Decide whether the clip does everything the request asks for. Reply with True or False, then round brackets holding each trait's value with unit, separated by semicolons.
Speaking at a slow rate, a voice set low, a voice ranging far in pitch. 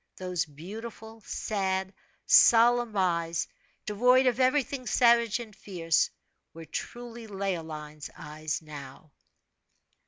False (95 wpm; 195 Hz; 6.2 semitones)